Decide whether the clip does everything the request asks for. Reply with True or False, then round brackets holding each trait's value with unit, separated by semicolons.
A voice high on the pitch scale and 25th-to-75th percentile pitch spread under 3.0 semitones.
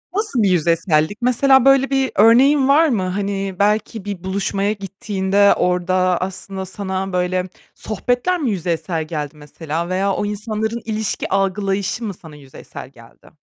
False (195 Hz; 3.3 semitones)